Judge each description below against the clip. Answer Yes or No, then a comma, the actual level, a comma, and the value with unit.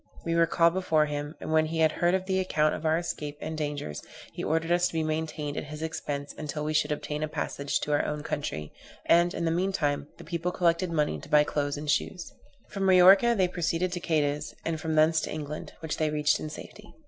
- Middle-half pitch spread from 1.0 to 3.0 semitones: Yes, narrow, 2.4 semitones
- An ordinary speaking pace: No, fast, 230 wpm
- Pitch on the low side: No, medium, 155 Hz